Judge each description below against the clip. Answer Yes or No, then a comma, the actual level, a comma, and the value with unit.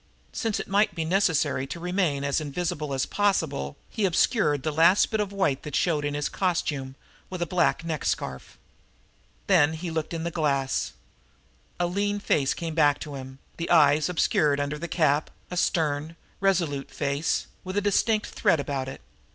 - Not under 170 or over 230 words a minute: Yes, average, 175 wpm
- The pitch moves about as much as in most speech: Yes, average, 3.9 semitones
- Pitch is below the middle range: No, medium, 160 Hz